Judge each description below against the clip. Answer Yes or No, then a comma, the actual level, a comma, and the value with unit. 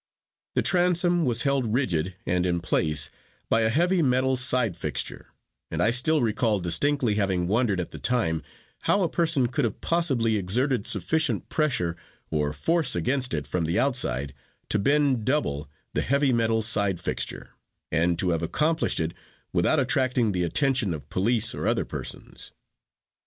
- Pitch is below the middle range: Yes, low, 115 Hz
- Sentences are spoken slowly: No, average, 160 wpm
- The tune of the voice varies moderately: No, wide, 7.5 semitones